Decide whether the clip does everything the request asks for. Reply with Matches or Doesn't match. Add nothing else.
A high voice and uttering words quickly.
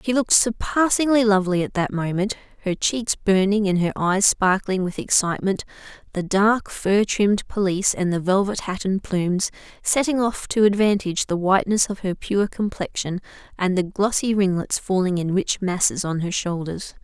Doesn't match